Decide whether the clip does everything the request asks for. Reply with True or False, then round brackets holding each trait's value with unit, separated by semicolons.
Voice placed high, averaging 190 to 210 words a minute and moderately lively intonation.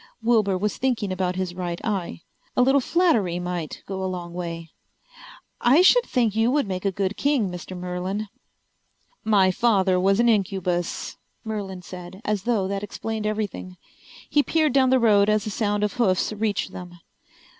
False (200 Hz; 170 wpm; 3.5 semitones)